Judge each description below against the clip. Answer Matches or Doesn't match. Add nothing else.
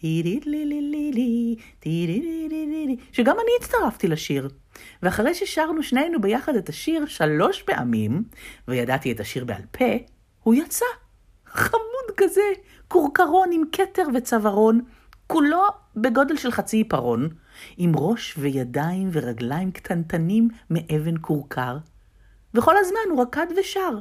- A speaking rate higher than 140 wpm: Doesn't match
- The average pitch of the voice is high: Matches